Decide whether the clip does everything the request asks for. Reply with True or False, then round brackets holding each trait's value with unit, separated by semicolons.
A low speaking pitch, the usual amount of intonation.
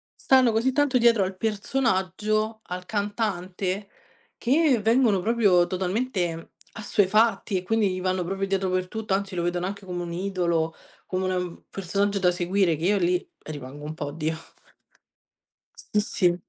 False (190 Hz; 3.2 semitones)